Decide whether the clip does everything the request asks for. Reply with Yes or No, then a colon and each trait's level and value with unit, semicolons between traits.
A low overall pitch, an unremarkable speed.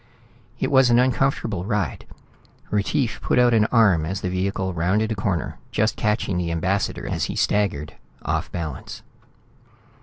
Yes: low, 100 Hz; average, 150 wpm